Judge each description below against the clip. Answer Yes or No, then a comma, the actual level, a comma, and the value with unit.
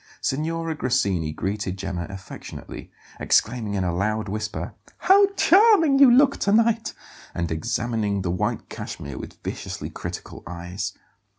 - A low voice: Yes, low, 110 Hz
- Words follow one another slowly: Yes, slow, 130 wpm